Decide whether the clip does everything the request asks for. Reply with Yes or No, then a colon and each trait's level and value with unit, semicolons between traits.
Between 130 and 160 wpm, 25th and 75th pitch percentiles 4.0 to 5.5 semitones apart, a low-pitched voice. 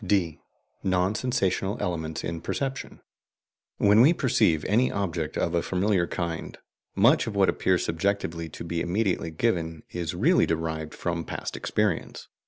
No: average, 145 wpm; average, 3.5 semitones; very low, 90 Hz